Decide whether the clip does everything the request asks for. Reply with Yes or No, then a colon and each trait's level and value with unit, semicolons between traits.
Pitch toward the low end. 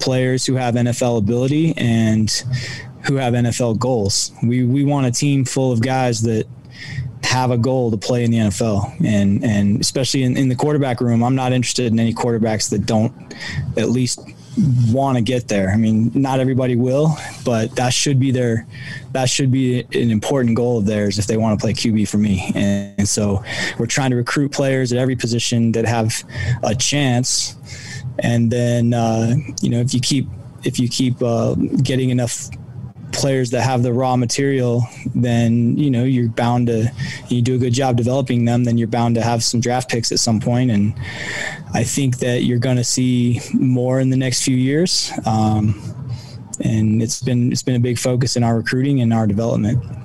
Yes: low, 120 Hz